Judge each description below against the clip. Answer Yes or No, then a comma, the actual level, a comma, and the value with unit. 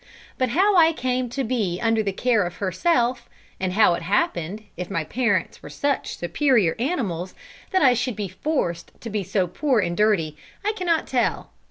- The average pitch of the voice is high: Yes, high, 220 Hz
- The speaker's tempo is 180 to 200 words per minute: Yes, average, 185 wpm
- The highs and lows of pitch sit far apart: Yes, wide, 6.0 semitones